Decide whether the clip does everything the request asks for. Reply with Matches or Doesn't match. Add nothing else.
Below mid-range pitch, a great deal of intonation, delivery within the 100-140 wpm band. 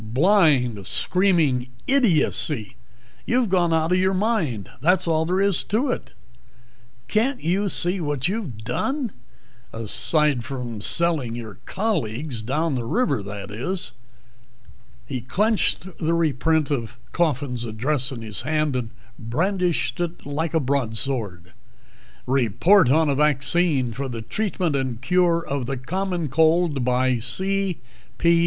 Doesn't match